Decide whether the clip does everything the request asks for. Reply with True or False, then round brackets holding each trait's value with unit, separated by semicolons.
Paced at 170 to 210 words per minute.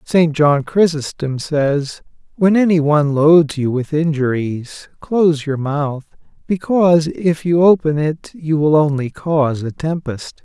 False (140 wpm)